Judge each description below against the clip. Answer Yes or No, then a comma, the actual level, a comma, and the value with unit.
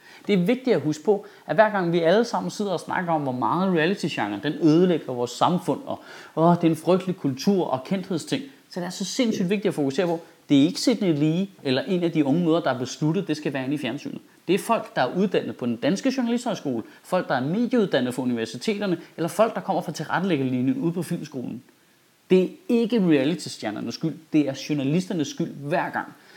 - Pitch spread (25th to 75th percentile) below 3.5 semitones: No, average, 4.9 semitones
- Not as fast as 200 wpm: No, fast, 225 wpm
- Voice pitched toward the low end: No, medium, 170 Hz